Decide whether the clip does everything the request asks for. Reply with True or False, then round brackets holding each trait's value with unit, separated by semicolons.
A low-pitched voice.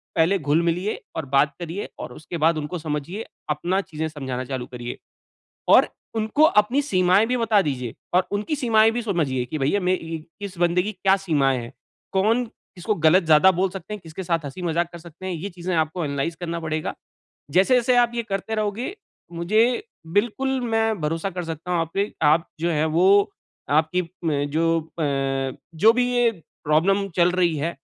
False (175 Hz)